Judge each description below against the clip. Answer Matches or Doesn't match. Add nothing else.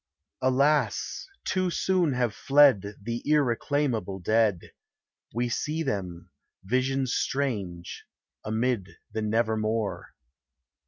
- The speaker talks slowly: Matches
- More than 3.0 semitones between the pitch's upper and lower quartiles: Matches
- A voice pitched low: Matches